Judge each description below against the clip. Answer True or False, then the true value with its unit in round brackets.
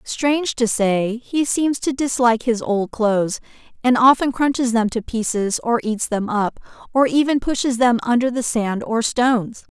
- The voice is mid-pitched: False (240 Hz)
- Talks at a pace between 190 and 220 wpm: False (180 wpm)